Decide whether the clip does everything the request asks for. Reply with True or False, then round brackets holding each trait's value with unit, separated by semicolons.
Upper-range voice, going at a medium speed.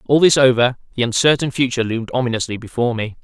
False (125 Hz; 185 wpm)